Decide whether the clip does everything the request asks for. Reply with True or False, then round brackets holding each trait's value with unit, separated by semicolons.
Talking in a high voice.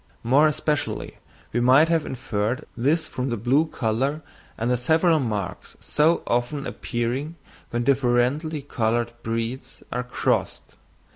False (125 Hz)